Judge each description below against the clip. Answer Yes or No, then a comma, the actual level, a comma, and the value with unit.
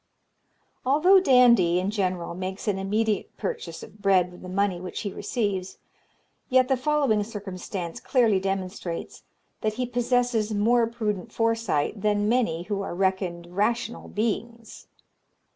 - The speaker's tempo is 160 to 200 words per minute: No, slow, 135 wpm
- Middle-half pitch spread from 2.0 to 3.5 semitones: No, average, 4.0 semitones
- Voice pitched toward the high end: Yes, high, 210 Hz